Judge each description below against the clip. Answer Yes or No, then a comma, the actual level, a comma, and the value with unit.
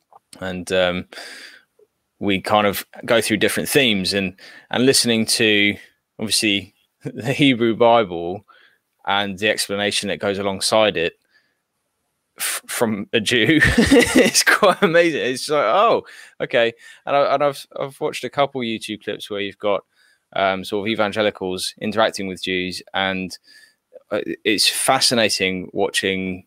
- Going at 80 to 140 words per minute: Yes, slow, 135 wpm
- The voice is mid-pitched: No, low, 105 Hz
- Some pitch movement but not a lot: No, wide, 5.7 semitones